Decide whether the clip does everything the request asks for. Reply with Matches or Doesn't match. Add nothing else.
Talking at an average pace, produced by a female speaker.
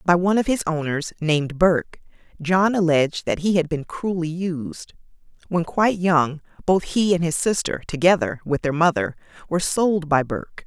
Matches